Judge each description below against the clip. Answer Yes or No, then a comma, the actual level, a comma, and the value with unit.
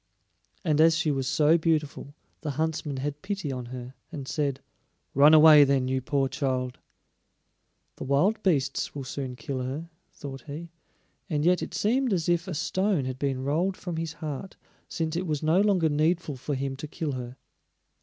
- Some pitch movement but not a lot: Yes, average, 3.5 semitones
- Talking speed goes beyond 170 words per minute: Yes, average, 180 wpm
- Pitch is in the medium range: Yes, medium, 150 Hz